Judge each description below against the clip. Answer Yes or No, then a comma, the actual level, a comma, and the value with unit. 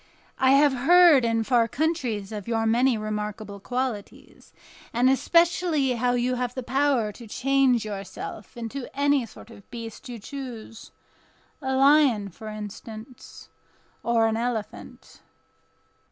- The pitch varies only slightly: No, average, 3.4 semitones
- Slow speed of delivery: Yes, slow, 125 wpm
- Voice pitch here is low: No, high, 240 Hz